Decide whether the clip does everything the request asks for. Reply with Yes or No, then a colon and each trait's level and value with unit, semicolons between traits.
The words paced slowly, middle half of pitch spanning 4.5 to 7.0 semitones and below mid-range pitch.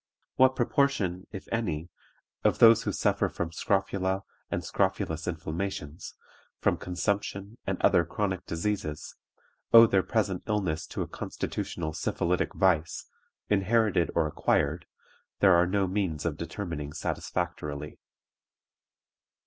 No: slow, 115 wpm; average, 3.7 semitones; very low, 90 Hz